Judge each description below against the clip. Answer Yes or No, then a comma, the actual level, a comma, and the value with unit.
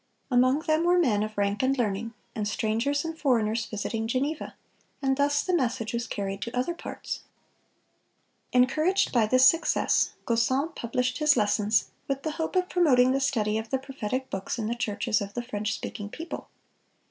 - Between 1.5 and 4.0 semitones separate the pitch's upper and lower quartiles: No, average, 4.6 semitones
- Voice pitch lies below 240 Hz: No, very high, 250 Hz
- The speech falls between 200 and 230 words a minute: No, average, 175 wpm